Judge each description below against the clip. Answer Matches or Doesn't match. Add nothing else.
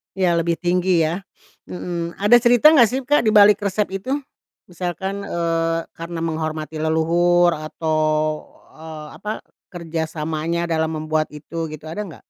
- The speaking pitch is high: Doesn't match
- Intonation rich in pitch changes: Doesn't match